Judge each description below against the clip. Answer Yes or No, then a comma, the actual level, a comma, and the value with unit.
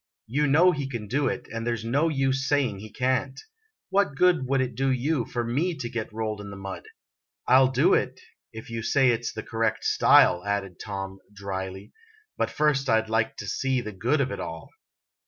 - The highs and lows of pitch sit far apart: No, average, 4.1 semitones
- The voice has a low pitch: Yes, low, 120 Hz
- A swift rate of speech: Yes, fast, 210 wpm